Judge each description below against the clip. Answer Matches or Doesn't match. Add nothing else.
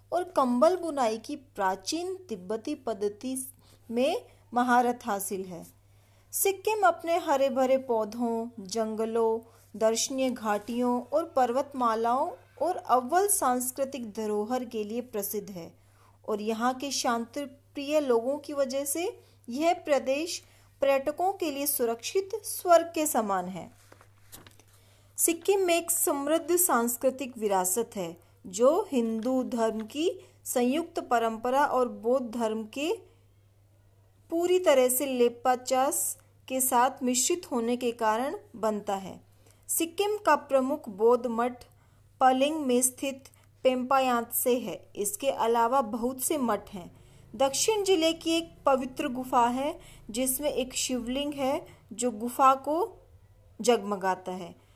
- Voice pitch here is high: Matches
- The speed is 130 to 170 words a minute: Doesn't match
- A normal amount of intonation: Matches